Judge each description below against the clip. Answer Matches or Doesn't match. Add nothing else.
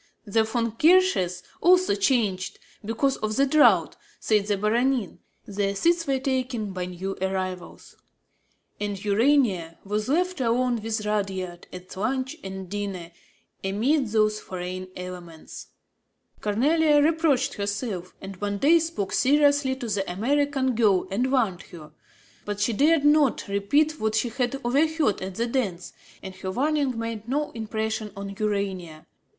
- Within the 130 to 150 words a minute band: Matches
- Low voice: Doesn't match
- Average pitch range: Doesn't match